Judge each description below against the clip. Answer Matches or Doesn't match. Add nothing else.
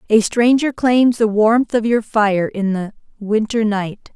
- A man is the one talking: Doesn't match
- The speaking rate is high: Doesn't match